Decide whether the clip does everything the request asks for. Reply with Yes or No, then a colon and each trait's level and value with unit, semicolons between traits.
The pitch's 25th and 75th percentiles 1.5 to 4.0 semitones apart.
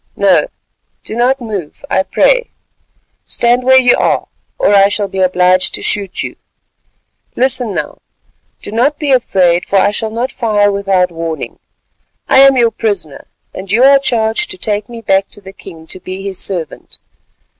No: average, 4.6 semitones